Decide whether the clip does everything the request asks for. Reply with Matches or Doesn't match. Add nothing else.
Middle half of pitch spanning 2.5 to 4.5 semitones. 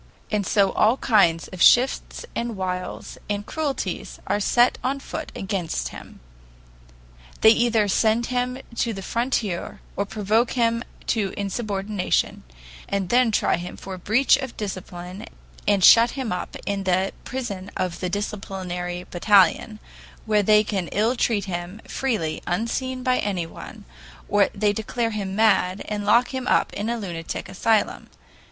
Matches